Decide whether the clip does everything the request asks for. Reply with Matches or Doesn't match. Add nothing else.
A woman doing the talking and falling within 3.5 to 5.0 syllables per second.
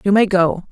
Doesn't match